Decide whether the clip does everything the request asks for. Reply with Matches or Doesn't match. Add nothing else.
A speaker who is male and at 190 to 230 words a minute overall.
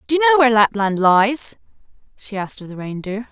Doesn't match